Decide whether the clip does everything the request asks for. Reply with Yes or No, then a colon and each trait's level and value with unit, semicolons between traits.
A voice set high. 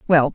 No: medium, 155 Hz